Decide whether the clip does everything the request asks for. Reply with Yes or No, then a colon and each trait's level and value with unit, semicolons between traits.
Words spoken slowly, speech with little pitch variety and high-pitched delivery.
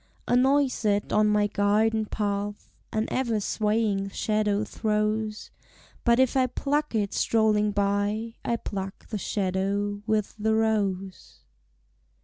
Yes: slow, 125 wpm; narrow, 1.6 semitones; high, 210 Hz